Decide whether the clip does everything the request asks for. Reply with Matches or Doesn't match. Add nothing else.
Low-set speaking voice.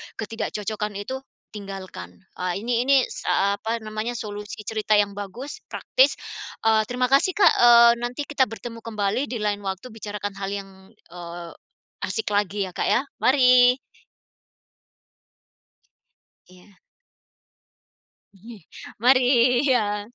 Doesn't match